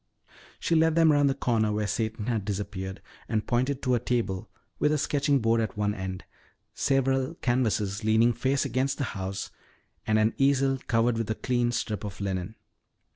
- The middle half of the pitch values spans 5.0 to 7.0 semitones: No, average, 4.2 semitones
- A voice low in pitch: Yes, low, 115 Hz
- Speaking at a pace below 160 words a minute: No, average, 180 wpm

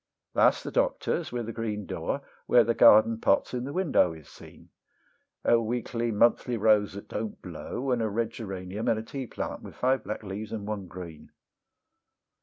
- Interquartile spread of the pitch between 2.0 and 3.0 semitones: Yes, narrow, 2.6 semitones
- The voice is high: No, low, 110 Hz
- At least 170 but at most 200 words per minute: Yes, average, 180 wpm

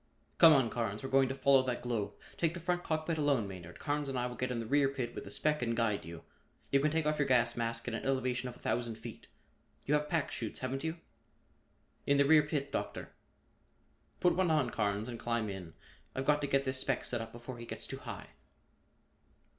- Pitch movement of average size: Yes, average, 3.9 semitones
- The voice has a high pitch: No, low, 130 Hz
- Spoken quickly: Yes, fast, 230 wpm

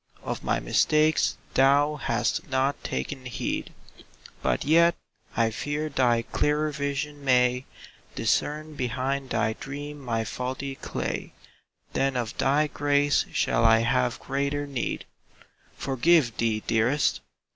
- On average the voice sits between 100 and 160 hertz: Yes, low, 135 Hz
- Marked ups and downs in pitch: No, average, 3.0 semitones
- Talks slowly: Yes, slow, 125 wpm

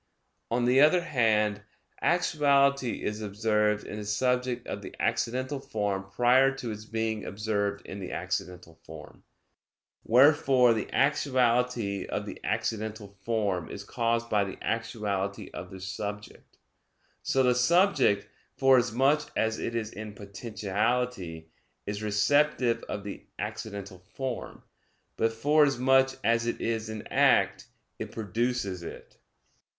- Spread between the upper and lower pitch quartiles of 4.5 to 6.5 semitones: No, average, 3.7 semitones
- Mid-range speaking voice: No, low, 115 Hz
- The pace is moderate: No, slow, 125 wpm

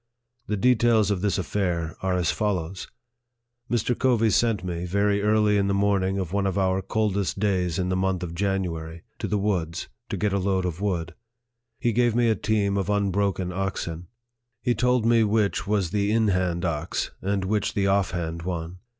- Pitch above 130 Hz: No, low, 100 Hz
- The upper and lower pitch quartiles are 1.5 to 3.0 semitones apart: Yes, narrow, 2.5 semitones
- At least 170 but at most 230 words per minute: Yes, average, 190 wpm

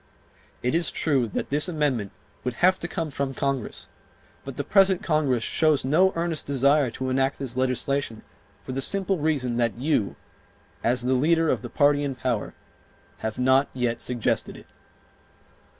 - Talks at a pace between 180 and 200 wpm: No, average, 165 wpm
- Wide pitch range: No, average, 3.6 semitones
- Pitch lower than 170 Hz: Yes, low, 135 Hz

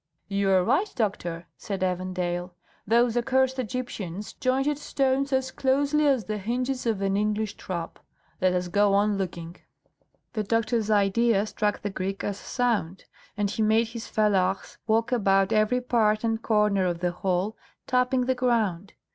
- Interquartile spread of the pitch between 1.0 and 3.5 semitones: No, average, 4.2 semitones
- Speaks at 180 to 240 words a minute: No, average, 155 wpm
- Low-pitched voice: No, high, 215 Hz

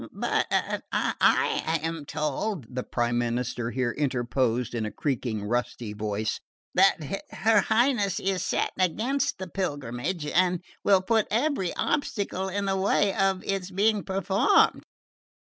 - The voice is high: No, medium, 180 Hz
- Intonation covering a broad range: Yes, wide, 8.1 semitones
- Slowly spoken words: Yes, slow, 130 wpm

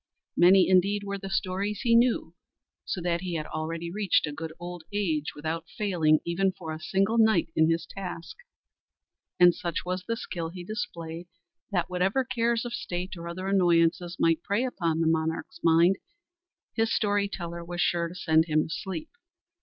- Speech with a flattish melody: No, average, 3.1 semitones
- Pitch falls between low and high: Yes, medium, 175 Hz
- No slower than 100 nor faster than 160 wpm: No, average, 175 wpm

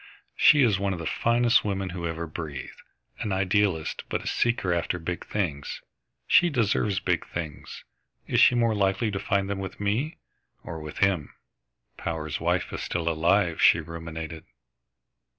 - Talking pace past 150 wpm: Yes, average, 165 wpm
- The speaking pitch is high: No, very low, 95 Hz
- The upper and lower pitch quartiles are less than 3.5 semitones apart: No, average, 3.9 semitones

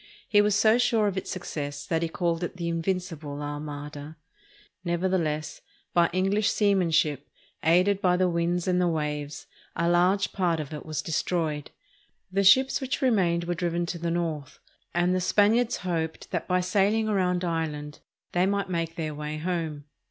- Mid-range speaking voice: Yes, medium, 175 Hz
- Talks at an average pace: Yes, average, 170 wpm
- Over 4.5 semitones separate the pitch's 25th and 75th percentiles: No, average, 3.1 semitones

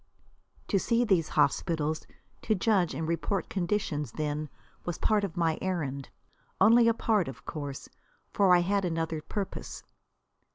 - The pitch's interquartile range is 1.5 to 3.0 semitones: No, average, 4.7 semitones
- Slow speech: No, average, 150 wpm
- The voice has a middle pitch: Yes, medium, 175 Hz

